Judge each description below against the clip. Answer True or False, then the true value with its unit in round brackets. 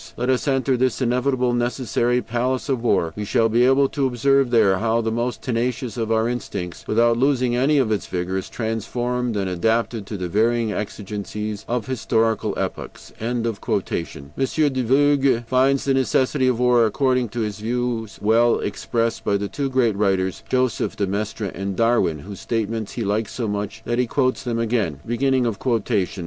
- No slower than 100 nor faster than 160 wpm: False (170 wpm)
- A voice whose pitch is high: False (115 Hz)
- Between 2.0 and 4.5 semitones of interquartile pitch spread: True (3.0 semitones)